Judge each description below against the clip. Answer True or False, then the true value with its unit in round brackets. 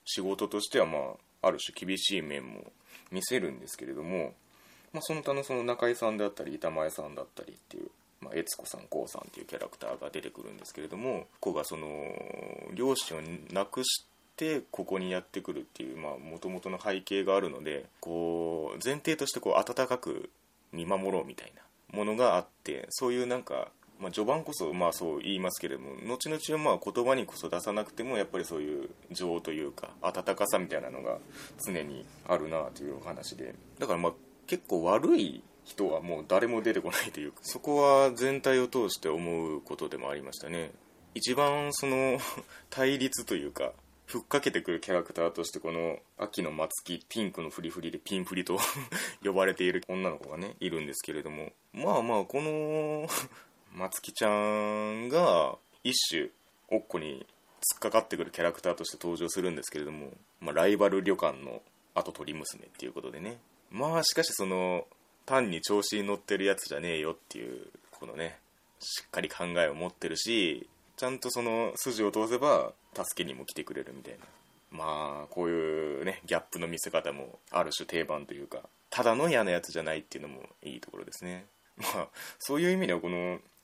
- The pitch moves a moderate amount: False (7.1 semitones)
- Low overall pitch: True (105 Hz)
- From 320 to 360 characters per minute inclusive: False (380 characters per minute)